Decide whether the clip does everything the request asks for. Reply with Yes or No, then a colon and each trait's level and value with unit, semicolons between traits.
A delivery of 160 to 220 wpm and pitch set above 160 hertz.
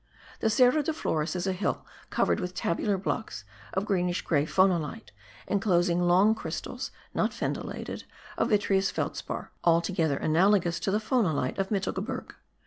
No: average, 140 wpm; high, 190 Hz